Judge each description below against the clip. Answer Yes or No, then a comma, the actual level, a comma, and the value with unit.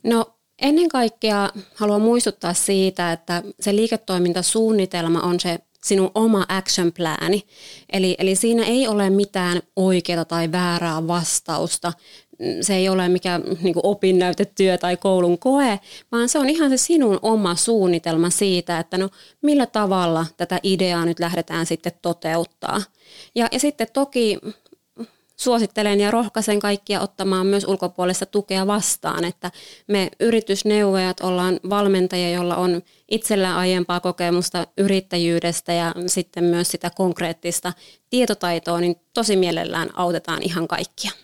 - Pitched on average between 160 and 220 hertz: Yes, medium, 185 Hz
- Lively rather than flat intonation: No, average, 3.2 semitones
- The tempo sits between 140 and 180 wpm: No, average, 130 wpm